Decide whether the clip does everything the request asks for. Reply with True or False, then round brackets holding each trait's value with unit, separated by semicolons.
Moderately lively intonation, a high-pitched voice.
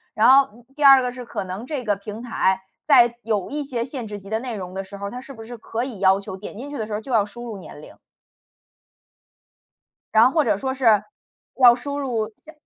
True (4.0 semitones; 230 Hz)